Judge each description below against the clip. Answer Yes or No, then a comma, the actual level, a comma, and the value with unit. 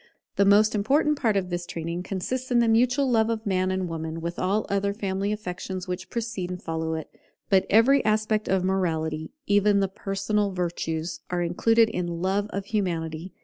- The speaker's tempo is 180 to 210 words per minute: Yes, average, 185 wpm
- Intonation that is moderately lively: Yes, average, 3.5 semitones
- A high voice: Yes, high, 195 Hz